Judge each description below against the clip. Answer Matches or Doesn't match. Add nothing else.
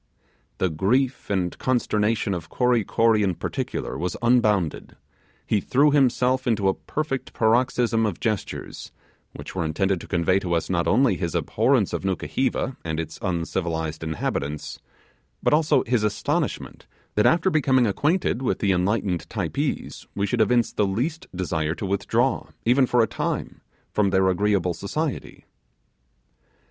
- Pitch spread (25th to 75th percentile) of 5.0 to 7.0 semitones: Matches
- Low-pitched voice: Matches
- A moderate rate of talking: Matches